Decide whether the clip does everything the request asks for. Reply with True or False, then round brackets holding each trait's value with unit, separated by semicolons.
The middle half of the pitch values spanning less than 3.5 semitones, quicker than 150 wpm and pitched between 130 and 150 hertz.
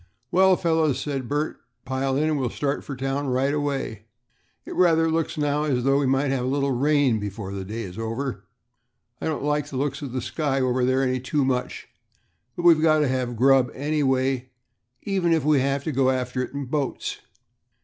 True (2.6 semitones; 200 wpm; 135 Hz)